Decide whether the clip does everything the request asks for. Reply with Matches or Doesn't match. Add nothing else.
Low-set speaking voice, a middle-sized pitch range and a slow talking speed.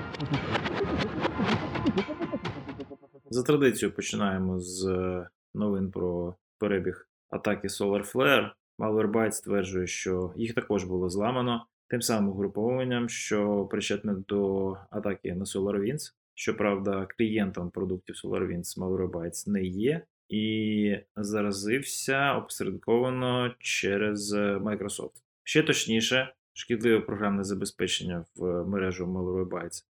Matches